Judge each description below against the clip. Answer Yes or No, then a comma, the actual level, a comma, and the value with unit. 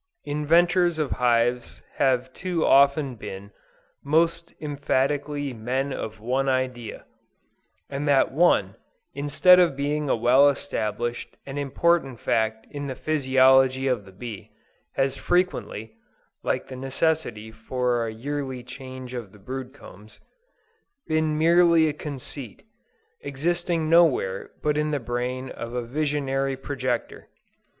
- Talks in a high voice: No, low, 135 Hz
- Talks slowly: Yes, slow, 125 wpm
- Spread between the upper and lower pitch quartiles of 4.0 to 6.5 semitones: No, average, 3.5 semitones